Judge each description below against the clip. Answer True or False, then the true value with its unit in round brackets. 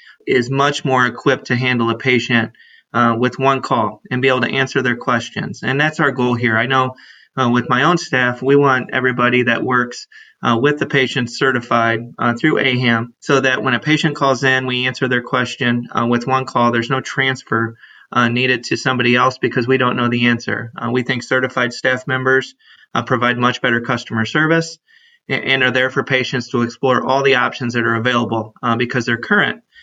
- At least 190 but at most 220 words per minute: True (205 wpm)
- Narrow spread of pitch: True (1.7 semitones)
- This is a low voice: True (125 Hz)